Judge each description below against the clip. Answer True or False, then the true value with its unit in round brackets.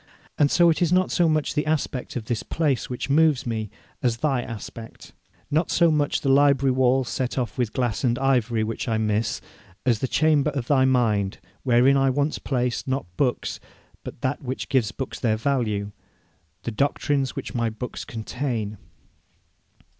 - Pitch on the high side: False (130 Hz)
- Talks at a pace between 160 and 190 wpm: True (175 wpm)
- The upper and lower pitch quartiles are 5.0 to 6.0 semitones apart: False (3.6 semitones)